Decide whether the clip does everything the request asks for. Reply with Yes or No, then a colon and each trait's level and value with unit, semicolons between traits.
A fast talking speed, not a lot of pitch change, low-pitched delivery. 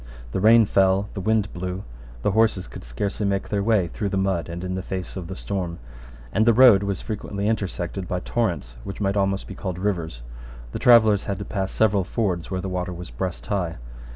Yes: fast, 210 wpm; narrow, 2.2 semitones; very low, 95 Hz